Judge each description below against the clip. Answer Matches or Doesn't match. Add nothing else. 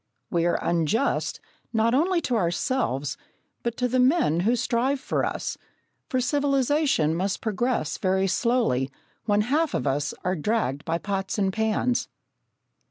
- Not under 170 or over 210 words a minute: Doesn't match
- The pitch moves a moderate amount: Doesn't match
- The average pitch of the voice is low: Doesn't match